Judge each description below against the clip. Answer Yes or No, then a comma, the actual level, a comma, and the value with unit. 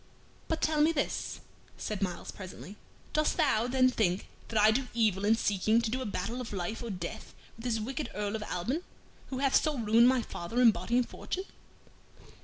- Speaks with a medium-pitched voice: No, high, 225 Hz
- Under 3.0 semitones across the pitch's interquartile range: No, average, 3.7 semitones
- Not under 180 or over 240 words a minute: Yes, average, 200 wpm